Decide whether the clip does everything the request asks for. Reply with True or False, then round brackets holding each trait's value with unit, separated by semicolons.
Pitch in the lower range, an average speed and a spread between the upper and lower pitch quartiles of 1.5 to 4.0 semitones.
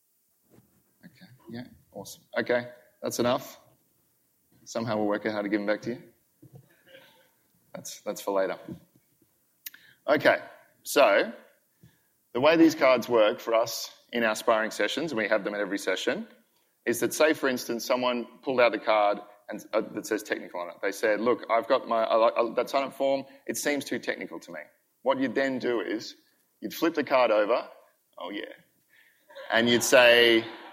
True (120 Hz; 175 wpm; 3.3 semitones)